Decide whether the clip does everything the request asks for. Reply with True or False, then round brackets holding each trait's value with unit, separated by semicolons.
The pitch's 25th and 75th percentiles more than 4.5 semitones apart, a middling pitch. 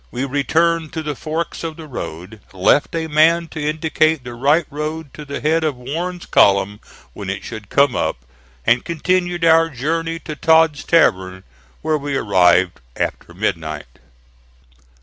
True (5.2 semitones; 150 Hz)